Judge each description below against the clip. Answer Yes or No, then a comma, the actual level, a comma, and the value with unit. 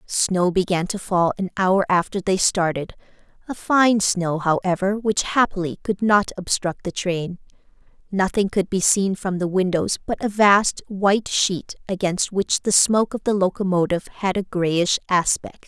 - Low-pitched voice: No, high, 190 Hz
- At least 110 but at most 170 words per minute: Yes, average, 165 wpm